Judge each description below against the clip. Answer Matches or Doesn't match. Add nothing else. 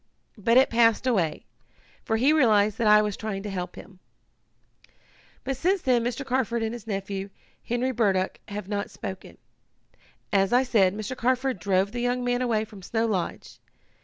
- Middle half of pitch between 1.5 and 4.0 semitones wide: Matches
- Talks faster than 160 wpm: Matches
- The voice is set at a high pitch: Matches